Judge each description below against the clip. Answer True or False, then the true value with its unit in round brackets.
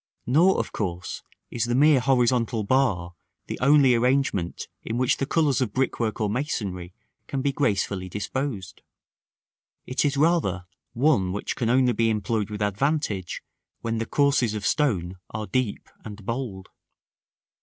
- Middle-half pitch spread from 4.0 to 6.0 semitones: True (4.9 semitones)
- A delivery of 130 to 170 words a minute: True (145 wpm)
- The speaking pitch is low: True (115 Hz)